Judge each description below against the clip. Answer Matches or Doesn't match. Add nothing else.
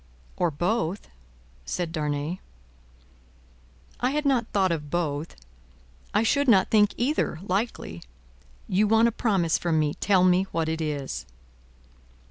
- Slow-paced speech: Matches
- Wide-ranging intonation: Matches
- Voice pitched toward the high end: Doesn't match